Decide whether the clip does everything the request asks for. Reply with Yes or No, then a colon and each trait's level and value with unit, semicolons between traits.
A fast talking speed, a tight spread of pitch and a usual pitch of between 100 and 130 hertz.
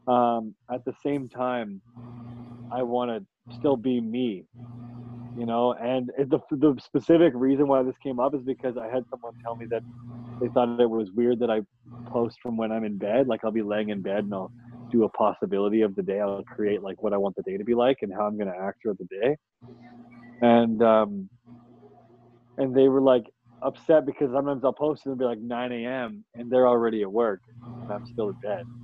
Yes: fast, 220 wpm; narrow, 1.8 semitones; low, 120 Hz